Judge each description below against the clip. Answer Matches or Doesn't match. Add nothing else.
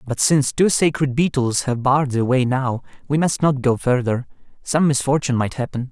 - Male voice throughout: Matches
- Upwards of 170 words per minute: Matches